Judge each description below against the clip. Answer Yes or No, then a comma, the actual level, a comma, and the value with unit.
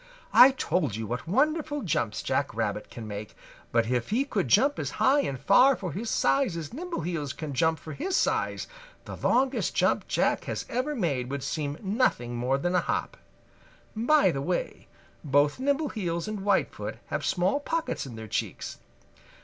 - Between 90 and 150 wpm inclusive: No, average, 175 wpm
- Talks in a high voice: No, medium, 180 Hz